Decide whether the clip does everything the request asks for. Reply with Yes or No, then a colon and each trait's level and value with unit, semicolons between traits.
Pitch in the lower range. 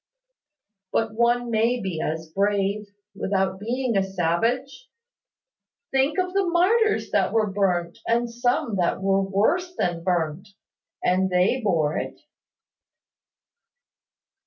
No: high, 205 Hz